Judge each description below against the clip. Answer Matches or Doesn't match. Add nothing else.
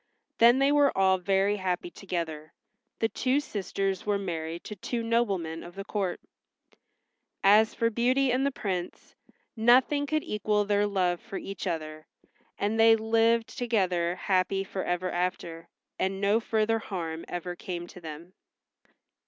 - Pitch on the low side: Doesn't match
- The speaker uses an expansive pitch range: Doesn't match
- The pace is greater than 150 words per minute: Doesn't match